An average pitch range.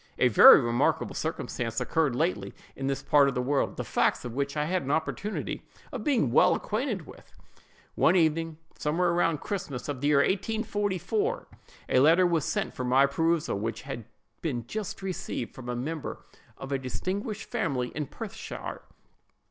No: wide, 6.0 semitones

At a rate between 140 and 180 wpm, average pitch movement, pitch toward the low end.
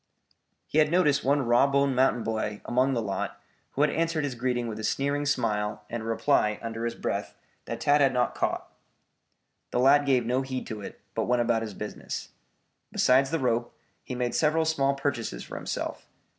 No: average, 195 wpm; average, 3.4 semitones; low, 125 Hz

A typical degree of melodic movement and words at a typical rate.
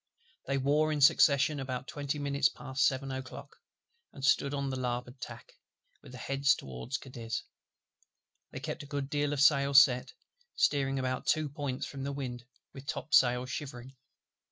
No: narrow, 1.8 semitones; average, 160 wpm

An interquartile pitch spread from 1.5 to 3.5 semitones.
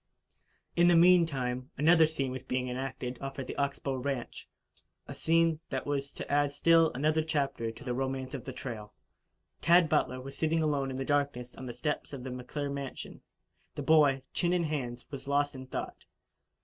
Yes: average, 3.1 semitones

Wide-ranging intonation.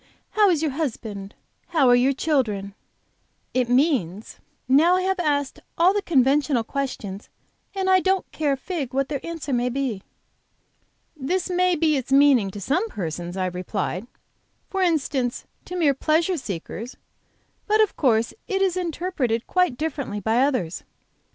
Yes: wide, 6.5 semitones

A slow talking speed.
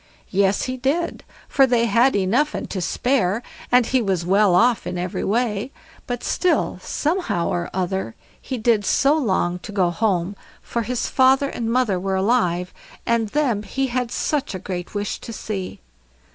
No: average, 175 wpm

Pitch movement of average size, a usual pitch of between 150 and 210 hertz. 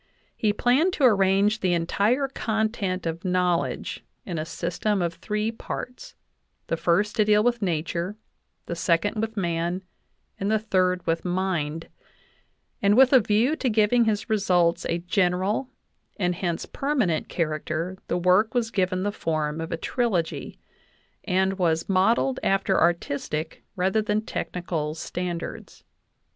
Yes: average, 4.0 semitones; high, 190 Hz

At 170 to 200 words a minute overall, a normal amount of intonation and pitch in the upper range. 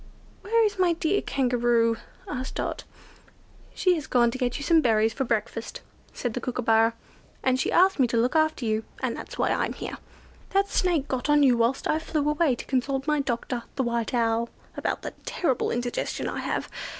Yes: average, 195 wpm; average, 4.6 semitones; very high, 255 Hz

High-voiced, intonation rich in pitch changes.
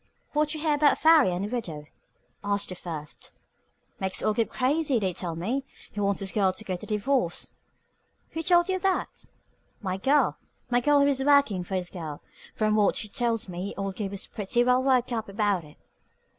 Yes: high, 215 Hz; wide, 6.4 semitones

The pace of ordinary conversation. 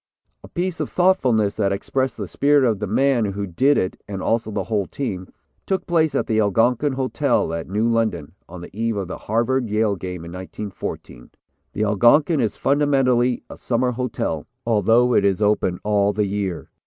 Yes: average, 185 wpm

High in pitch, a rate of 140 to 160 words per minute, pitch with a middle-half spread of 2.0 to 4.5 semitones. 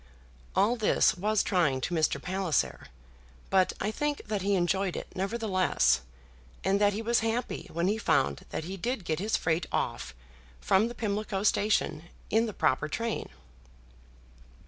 Yes: high, 195 Hz; average, 155 wpm; average, 3.9 semitones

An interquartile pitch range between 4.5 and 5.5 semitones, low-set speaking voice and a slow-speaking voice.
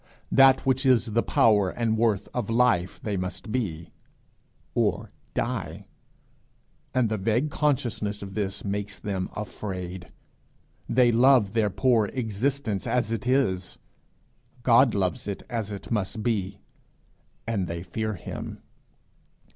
No: average, 3.8 semitones; low, 110 Hz; slow, 130 wpm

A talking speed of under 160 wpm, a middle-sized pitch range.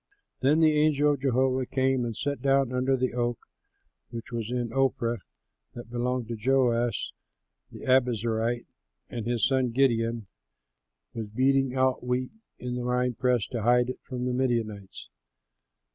No: average, 150 wpm; narrow, 1.9 semitones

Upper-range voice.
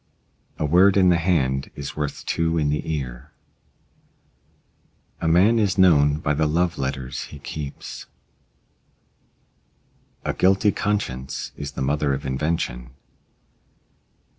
No: very low, 75 Hz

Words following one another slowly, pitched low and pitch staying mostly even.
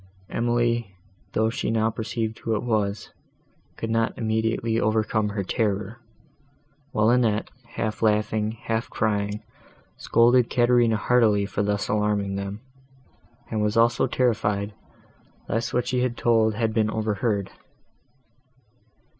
Yes: slow, 120 wpm; low, 110 Hz; narrow, 1.7 semitones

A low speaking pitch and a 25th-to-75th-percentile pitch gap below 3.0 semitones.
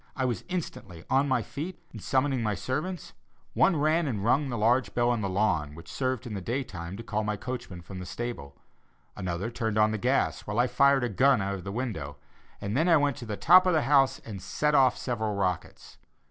No: low, 120 Hz; average, 5.1 semitones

